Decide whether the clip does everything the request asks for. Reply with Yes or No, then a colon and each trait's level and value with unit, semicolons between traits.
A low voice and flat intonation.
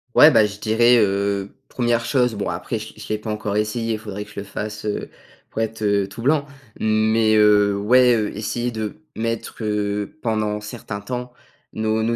Yes: low, 110 Hz; narrow, 1.9 semitones